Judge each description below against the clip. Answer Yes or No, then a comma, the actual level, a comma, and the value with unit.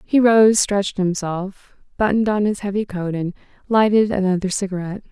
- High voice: Yes, high, 200 Hz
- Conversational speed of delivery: Yes, average, 155 wpm